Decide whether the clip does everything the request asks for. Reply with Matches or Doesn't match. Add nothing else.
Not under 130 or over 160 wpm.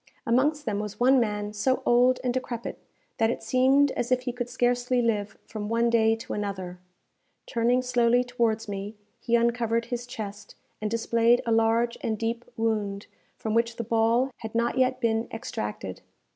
Doesn't match